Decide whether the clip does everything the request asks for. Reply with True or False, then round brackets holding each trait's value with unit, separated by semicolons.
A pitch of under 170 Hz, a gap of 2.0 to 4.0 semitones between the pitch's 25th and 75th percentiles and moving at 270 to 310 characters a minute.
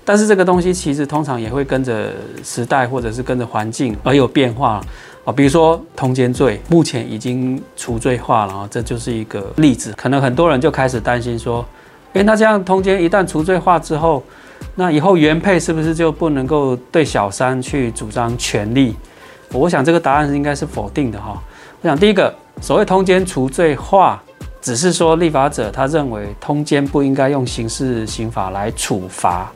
False (135 Hz; 5.2 semitones; 290 characters per minute)